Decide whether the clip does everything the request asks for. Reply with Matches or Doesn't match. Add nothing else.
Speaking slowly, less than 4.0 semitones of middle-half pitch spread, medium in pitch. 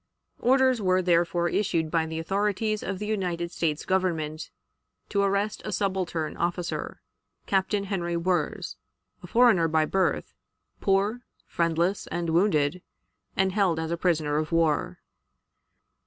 Matches